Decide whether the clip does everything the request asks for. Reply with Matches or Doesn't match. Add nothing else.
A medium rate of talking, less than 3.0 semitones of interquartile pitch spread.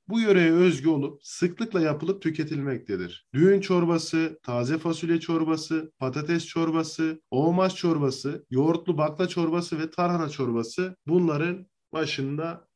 Matches